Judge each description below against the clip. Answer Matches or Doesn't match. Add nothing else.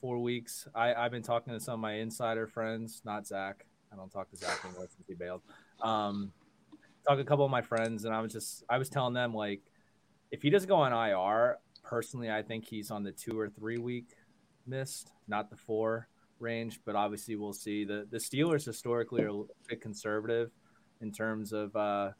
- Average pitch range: Doesn't match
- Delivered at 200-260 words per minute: Matches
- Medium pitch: Doesn't match